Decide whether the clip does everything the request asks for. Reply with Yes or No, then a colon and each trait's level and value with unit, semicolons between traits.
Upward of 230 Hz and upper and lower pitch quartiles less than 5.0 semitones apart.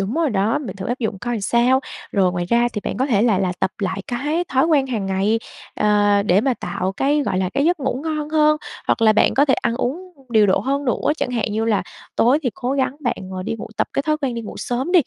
No: high, 240 Hz; average, 5.3 semitones